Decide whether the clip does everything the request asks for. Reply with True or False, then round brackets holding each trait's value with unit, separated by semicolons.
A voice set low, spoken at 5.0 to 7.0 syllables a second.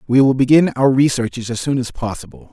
True (125 Hz; 6.0 syllables/s)